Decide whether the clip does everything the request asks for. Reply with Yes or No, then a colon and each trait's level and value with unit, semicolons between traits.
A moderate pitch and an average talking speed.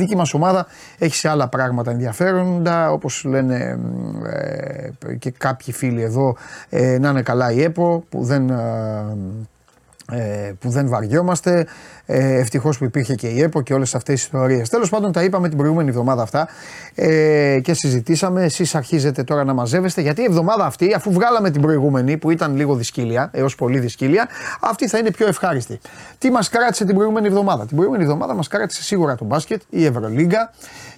No: medium, 150 Hz; fast, 175 wpm